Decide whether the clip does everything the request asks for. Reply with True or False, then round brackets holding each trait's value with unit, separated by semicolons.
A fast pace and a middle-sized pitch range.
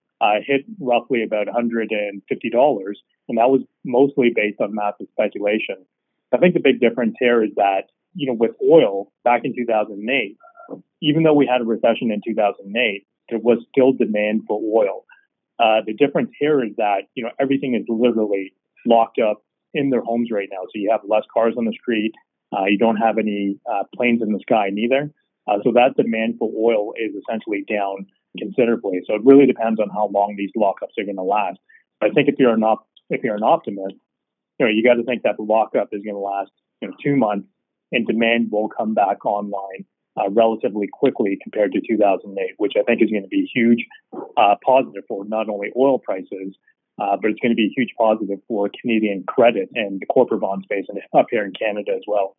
True (210 wpm; 3.3 semitones)